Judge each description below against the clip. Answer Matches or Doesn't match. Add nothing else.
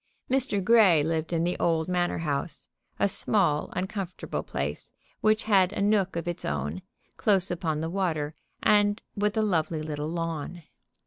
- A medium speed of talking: Matches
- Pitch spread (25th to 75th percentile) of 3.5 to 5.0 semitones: Matches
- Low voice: Doesn't match